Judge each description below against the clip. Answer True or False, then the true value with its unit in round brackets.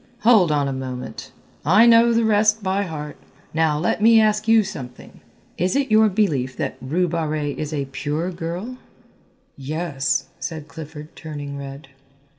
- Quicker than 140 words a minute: True (155 wpm)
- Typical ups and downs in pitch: False (6.4 semitones)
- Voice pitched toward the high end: False (160 Hz)